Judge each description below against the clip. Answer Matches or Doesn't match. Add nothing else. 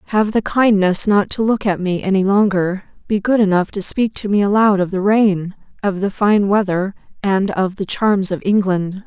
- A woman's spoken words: Matches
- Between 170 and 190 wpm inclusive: Doesn't match